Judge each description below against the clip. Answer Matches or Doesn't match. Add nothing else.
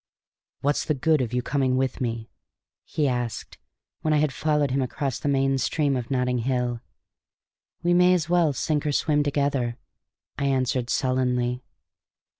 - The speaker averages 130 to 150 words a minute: Doesn't match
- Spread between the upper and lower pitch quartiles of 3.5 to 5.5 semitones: Doesn't match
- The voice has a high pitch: Doesn't match